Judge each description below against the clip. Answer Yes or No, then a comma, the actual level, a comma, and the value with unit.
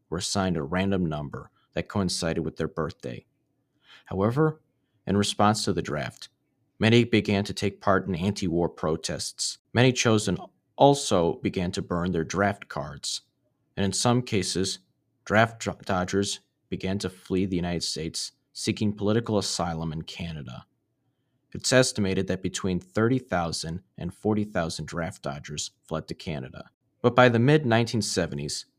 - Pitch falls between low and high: No, low, 100 Hz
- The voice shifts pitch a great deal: No, average, 4.3 semitones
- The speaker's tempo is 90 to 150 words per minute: Yes, average, 140 wpm